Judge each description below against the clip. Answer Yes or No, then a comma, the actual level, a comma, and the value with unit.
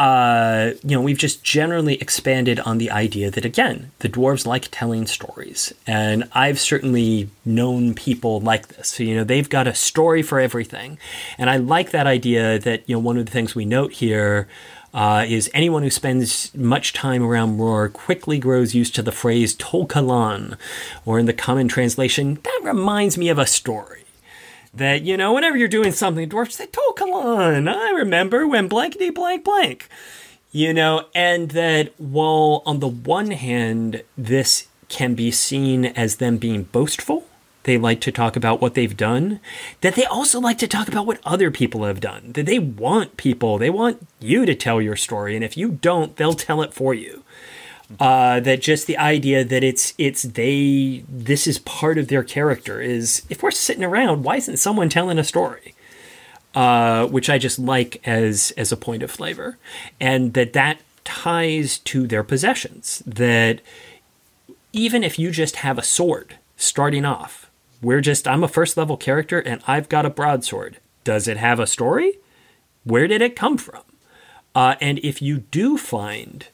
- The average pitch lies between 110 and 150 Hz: Yes, low, 135 Hz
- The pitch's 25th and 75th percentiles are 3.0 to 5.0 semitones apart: No, wide, 5.4 semitones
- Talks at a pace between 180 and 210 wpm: Yes, average, 185 wpm